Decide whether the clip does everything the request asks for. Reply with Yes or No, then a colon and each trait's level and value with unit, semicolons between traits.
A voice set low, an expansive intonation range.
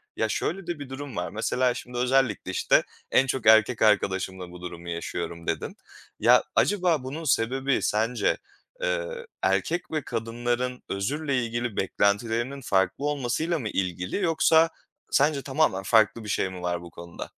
Yes: low, 120 Hz; wide, 6.6 semitones